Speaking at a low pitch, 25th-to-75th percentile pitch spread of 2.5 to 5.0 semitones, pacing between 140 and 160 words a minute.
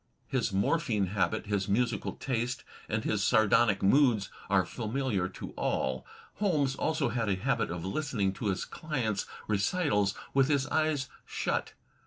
No: low, 110 Hz; wide, 5.4 semitones; average, 145 wpm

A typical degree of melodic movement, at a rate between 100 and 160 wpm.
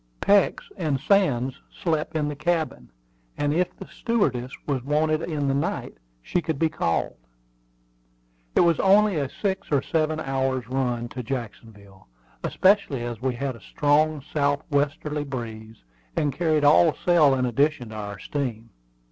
Yes: average, 4.0 semitones; average, 155 wpm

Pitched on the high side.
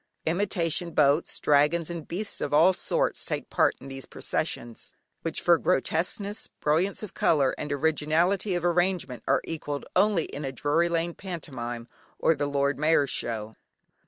No: medium, 160 Hz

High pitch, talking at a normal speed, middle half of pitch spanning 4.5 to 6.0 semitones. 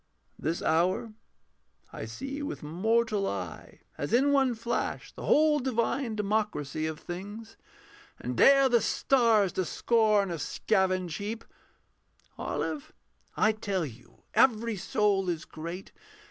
No: high, 215 Hz; slow, 125 wpm; average, 4.9 semitones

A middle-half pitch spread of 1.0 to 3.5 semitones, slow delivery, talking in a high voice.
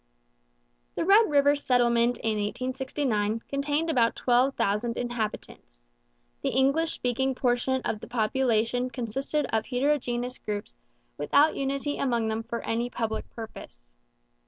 Yes: average, 3.2 semitones; slow, 125 wpm; high, 245 Hz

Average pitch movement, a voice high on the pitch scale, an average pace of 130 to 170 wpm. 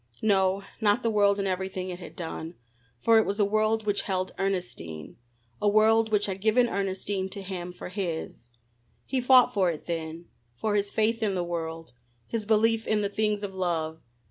No: average, 3.1 semitones; high, 200 Hz; average, 190 wpm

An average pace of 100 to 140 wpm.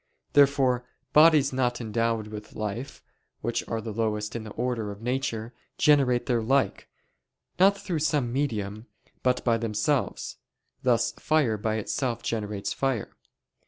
Yes: slow, 135 wpm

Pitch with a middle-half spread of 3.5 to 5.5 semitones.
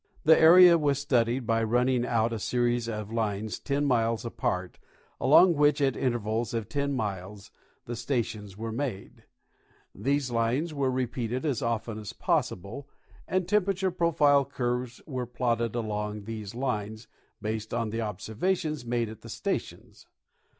Yes: average, 4.2 semitones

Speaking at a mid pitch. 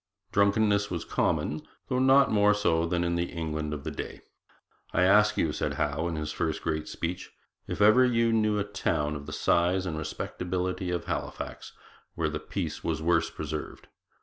No: very low, 85 Hz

